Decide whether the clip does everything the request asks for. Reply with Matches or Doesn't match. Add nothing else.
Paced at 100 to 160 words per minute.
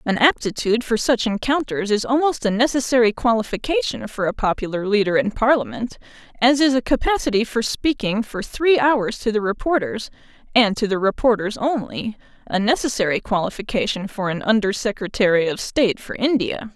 Matches